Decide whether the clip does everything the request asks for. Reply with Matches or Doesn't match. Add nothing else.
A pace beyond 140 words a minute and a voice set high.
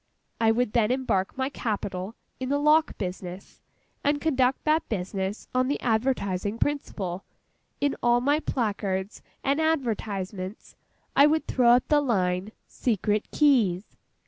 Doesn't match